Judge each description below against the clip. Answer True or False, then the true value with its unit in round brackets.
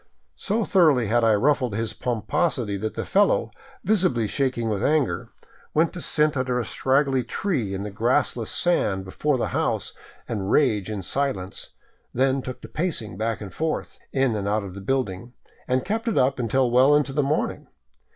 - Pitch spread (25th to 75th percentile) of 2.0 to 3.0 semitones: False (5.3 semitones)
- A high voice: False (125 Hz)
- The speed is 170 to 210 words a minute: True (180 wpm)